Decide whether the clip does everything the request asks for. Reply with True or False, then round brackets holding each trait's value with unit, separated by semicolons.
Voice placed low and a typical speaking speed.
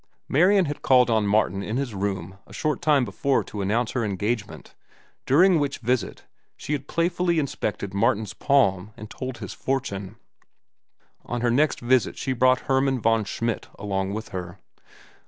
True (120 Hz; 160 wpm)